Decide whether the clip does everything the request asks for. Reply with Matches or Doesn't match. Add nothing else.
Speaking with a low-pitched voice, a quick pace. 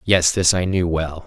Matches